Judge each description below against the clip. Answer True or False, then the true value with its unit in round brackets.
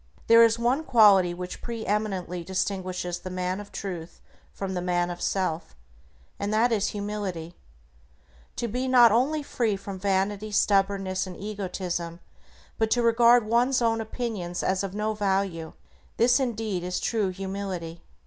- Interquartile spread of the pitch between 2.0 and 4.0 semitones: True (3.6 semitones)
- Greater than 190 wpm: False (150 wpm)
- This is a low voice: False (200 Hz)